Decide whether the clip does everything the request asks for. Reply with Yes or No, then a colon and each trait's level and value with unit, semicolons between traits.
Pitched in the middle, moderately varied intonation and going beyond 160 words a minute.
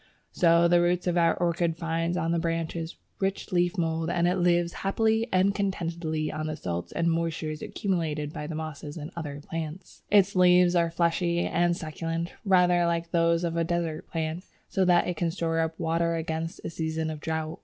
No: medium, 170 Hz; narrow, 1.5 semitones; average, 190 wpm